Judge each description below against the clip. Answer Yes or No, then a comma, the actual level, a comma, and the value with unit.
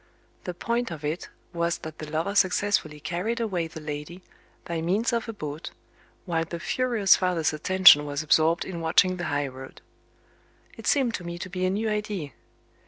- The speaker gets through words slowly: No, average, 180 wpm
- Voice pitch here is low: No, medium, 175 Hz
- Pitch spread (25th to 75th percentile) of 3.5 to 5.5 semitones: Yes, average, 4.1 semitones